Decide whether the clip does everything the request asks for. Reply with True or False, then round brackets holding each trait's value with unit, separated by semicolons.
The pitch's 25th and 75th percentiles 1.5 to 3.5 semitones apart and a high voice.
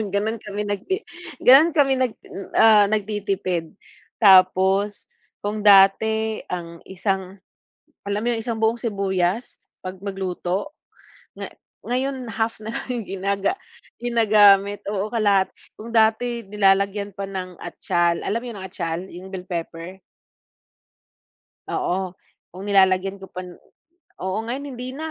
True (2.8 semitones; 200 Hz)